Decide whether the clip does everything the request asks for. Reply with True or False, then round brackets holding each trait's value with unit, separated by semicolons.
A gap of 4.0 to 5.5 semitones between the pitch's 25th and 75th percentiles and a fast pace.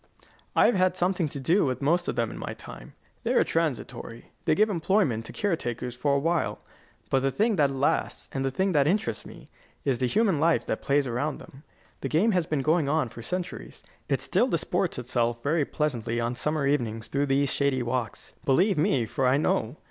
True (5.0 semitones; 210 wpm)